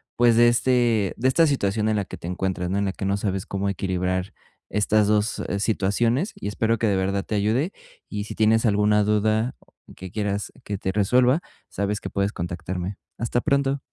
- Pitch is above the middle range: No, low, 105 Hz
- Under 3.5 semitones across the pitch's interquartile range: Yes, average, 2.8 semitones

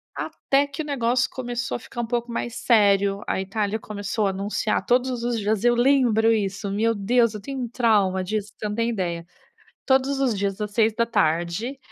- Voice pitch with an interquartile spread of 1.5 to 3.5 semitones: Yes, average, 3.1 semitones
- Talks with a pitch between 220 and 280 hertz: Yes, high, 225 Hz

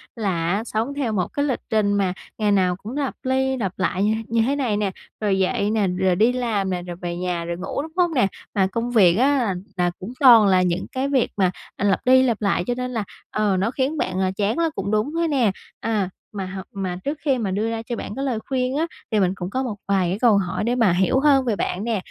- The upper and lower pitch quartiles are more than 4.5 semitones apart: Yes, average, 4.9 semitones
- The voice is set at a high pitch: Yes, high, 215 Hz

